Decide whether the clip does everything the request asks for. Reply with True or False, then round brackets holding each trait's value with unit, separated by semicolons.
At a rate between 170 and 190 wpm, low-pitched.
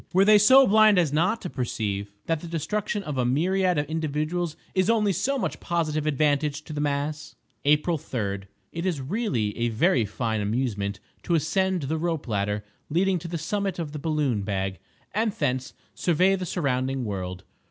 False (175 wpm; 155 Hz)